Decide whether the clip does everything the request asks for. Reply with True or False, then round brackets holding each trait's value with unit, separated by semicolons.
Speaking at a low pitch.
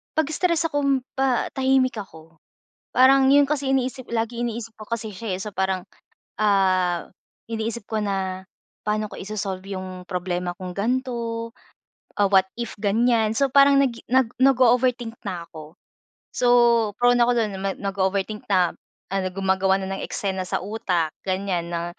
False (215 Hz)